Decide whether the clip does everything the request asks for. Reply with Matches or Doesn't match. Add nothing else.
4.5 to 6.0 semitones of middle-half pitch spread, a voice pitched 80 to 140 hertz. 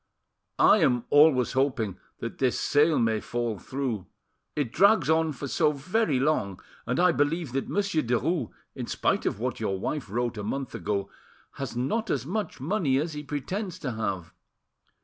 Matches